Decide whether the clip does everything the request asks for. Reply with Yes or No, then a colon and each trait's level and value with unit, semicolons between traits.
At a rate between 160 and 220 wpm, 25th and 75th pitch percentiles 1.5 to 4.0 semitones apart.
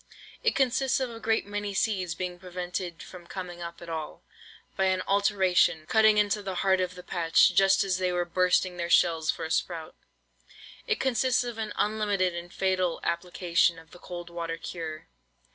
Yes: average, 180 wpm; average, 2.9 semitones